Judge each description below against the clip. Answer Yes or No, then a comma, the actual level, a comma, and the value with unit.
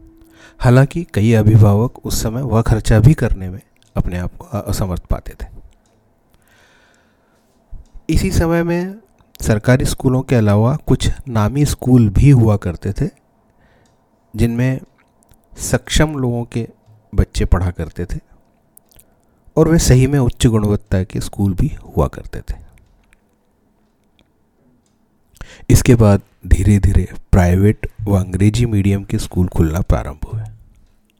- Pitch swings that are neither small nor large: Yes, average, 4.1 semitones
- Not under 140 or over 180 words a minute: No, average, 120 wpm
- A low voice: Yes, low, 110 Hz